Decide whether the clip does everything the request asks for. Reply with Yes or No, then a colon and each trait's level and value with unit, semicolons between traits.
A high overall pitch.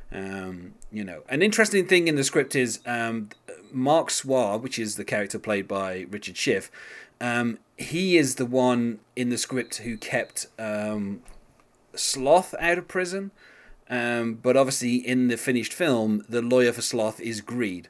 No: low, 120 Hz